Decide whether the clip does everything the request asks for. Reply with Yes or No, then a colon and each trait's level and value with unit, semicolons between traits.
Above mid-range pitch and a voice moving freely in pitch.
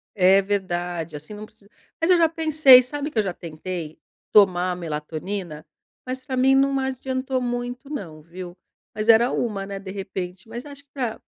Yes: high, 210 Hz; wide, 6.4 semitones